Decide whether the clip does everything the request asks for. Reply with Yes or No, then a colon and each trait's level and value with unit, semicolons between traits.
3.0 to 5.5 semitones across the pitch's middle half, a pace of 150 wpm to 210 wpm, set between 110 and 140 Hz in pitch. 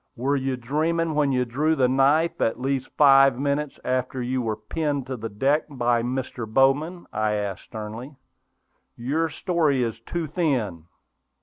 Yes: average, 3.8 semitones; average, 160 wpm; low, 135 Hz